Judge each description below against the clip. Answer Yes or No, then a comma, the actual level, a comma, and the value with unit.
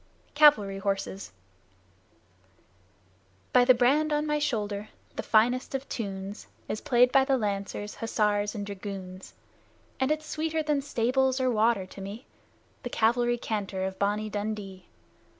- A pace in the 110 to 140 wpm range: Yes, slow, 135 wpm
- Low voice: No, high, 220 Hz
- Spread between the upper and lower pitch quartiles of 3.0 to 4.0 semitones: No, average, 4.6 semitones